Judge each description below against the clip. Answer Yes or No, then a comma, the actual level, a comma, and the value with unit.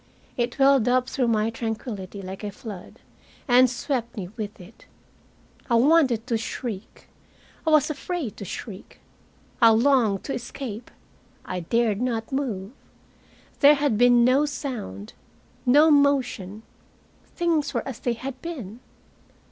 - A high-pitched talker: Yes, high, 240 Hz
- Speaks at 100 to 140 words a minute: Yes, slow, 135 wpm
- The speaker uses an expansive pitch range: No, average, 4.3 semitones